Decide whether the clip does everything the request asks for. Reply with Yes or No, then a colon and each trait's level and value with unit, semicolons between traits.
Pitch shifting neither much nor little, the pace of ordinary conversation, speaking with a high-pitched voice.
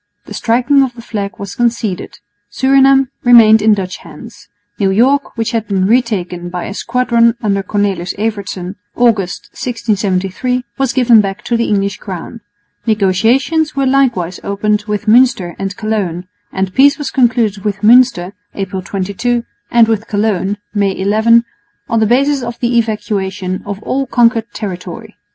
Yes: average, 3.6 semitones; average, 150 wpm; high, 215 Hz